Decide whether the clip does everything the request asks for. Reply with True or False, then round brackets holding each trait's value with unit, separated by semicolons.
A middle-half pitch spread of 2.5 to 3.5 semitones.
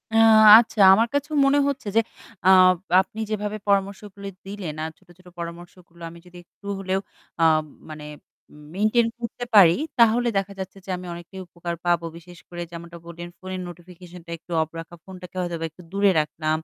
True (3.0 semitones)